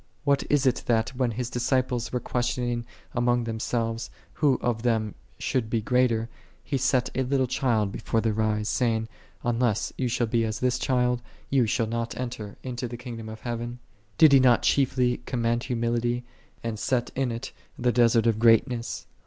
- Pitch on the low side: Yes, low, 120 Hz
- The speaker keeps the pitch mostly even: Yes, narrow, 1.7 semitones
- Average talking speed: Yes, average, 180 wpm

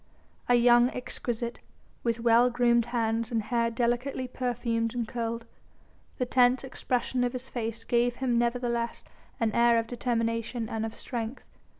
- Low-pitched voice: No, high, 235 Hz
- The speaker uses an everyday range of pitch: No, narrow, 1.2 semitones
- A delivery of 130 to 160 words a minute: Yes, average, 150 wpm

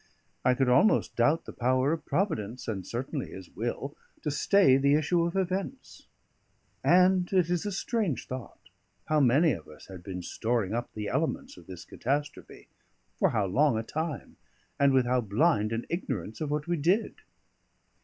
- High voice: No, medium, 140 Hz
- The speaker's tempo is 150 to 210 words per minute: Yes, average, 175 wpm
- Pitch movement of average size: No, wide, 6.6 semitones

